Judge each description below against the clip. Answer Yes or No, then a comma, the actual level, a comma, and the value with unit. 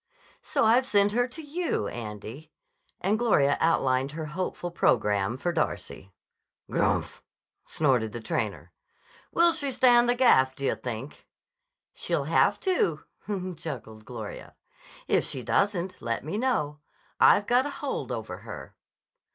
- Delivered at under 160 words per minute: Yes, slow, 135 wpm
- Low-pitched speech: No, medium, 165 Hz